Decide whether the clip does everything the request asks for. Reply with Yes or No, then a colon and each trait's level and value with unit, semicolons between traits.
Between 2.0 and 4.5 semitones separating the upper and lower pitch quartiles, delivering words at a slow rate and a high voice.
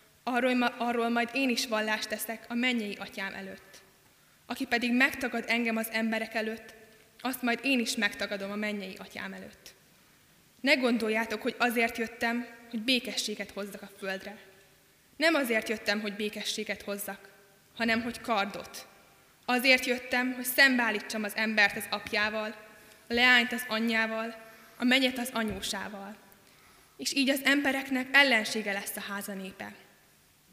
No: average, 2.7 semitones; average, 135 wpm; high, 225 Hz